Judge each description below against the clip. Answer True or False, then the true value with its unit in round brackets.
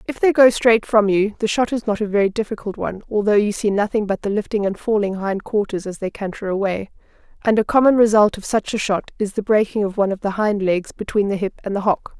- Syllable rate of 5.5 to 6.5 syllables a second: True (6.0 syllables/s)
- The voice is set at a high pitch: True (205 Hz)